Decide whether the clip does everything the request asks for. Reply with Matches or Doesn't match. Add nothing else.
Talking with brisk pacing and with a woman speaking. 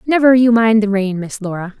Matches